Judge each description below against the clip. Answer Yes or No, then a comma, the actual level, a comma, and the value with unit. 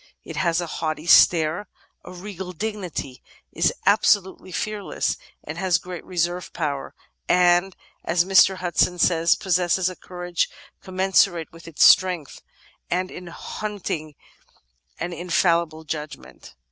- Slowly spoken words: Yes, slow, 125 wpm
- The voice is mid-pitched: Yes, medium, 175 Hz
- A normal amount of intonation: No, narrow, 2.1 semitones